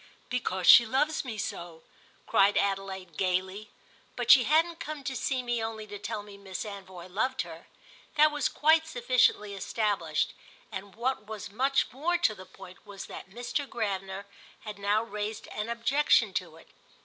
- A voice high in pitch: Yes, high, 215 Hz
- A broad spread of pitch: No, average, 4.7 semitones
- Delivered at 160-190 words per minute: Yes, average, 165 wpm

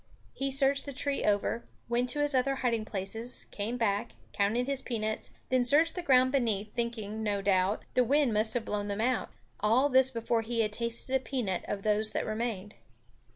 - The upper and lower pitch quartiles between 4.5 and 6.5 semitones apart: No, average, 3.5 semitones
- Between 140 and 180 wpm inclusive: No, average, 195 wpm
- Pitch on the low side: No, high, 235 Hz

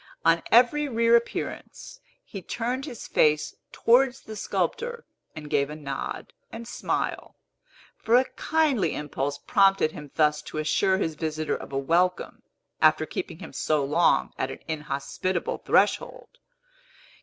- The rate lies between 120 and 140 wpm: Yes, slow, 135 wpm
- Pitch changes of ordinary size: No, wide, 7.7 semitones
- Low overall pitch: No, medium, 175 Hz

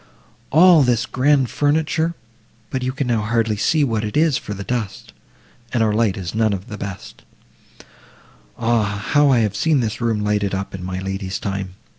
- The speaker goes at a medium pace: Yes, average, 180 wpm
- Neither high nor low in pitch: No, low, 115 Hz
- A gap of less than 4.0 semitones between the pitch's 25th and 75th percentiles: No, average, 4.7 semitones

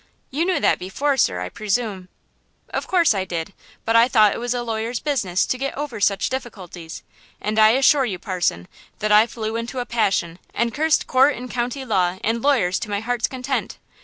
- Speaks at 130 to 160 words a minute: No, average, 200 wpm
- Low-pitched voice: No, high, 230 Hz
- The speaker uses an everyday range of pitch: Yes, average, 4.7 semitones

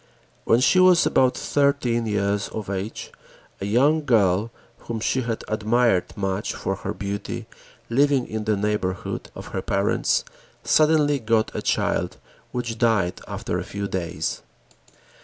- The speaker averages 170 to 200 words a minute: No, average, 140 wpm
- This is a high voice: No, low, 110 Hz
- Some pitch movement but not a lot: Yes, average, 4.1 semitones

